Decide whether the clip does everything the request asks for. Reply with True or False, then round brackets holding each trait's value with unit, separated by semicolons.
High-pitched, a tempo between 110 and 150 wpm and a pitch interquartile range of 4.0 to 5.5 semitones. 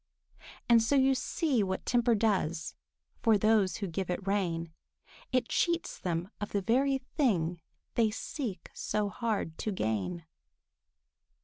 True (210 Hz; 135 wpm; 5.0 semitones)